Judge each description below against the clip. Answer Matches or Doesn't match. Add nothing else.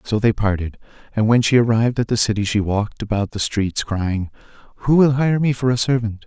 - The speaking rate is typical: Doesn't match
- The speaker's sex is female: Doesn't match